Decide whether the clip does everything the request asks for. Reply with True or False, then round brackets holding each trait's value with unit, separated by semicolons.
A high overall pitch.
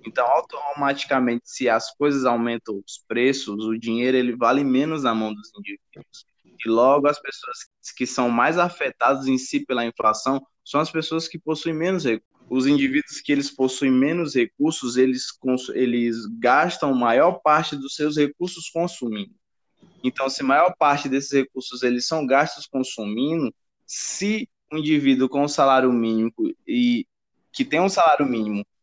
False (135 Hz)